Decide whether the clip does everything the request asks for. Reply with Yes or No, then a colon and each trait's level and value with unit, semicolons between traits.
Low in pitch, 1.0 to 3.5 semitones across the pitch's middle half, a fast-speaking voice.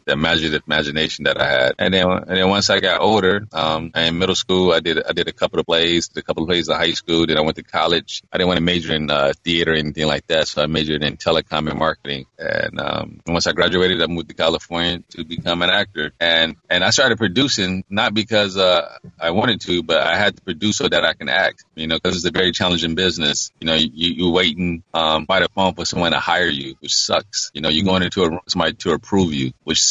Yes: very low, 85 Hz; average, 2.7 semitones; fast, 260 wpm